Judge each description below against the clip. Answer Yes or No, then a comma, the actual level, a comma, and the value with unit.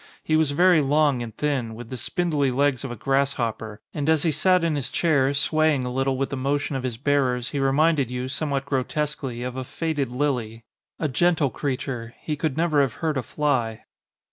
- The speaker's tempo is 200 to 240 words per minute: Yes, fast, 205 wpm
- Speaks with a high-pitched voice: No, medium, 140 Hz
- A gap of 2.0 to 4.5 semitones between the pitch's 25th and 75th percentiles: Yes, average, 3.2 semitones